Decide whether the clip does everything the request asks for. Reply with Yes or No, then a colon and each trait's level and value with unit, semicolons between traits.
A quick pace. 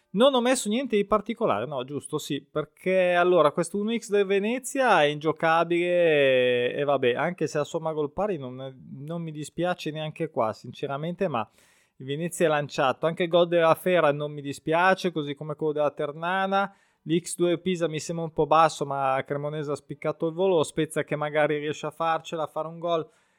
Yes: fast, 190 wpm